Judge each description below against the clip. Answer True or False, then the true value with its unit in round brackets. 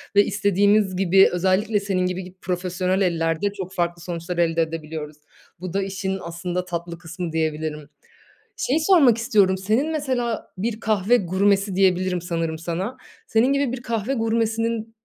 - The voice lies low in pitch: False (190 Hz)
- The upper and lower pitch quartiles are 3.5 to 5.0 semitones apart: True (4.1 semitones)